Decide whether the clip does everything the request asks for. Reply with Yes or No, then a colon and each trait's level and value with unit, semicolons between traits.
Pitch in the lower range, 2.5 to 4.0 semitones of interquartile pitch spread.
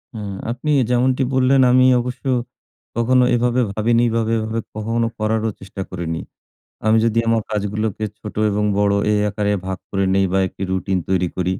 Yes: low, 110 Hz; average, 2.9 semitones